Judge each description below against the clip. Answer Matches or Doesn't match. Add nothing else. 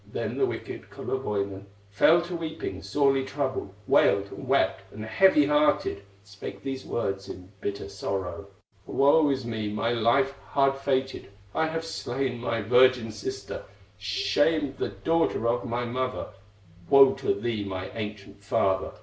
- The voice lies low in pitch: Matches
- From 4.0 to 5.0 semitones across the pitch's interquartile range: Doesn't match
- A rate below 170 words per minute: Matches